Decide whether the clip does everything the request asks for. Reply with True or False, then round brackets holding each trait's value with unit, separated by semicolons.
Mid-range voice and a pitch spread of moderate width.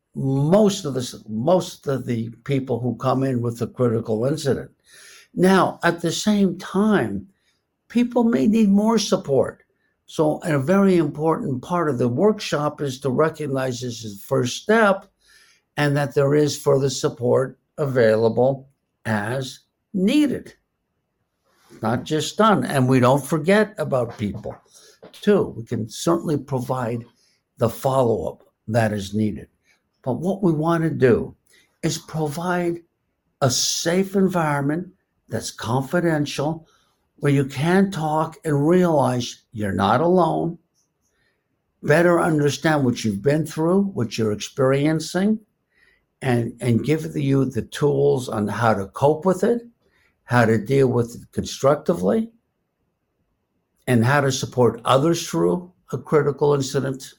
False (145 Hz; 5.7 semitones)